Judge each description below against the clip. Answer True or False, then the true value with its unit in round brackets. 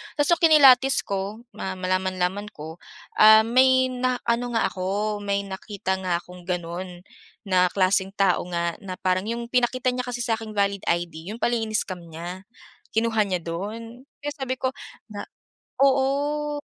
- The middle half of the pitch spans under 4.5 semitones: False (5.1 semitones)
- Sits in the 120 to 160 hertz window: False (210 Hz)